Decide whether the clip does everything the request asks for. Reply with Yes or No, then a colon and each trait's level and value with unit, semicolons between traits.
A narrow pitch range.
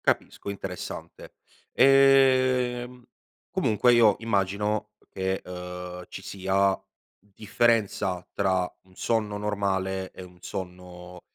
No: average, 3.8 semitones